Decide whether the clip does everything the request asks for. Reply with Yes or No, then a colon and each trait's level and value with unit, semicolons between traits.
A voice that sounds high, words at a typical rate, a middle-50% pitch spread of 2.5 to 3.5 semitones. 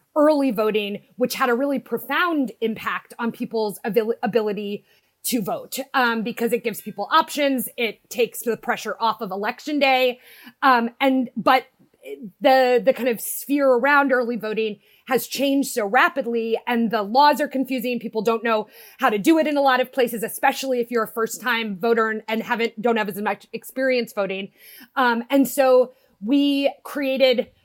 Yes: high, 245 Hz; average, 175 wpm; average, 2.9 semitones